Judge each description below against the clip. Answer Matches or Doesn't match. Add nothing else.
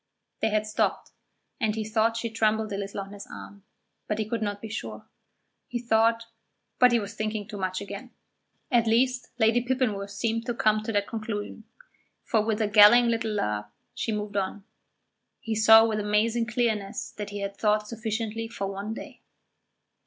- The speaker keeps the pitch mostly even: Matches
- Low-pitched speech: Doesn't match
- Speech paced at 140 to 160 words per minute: Doesn't match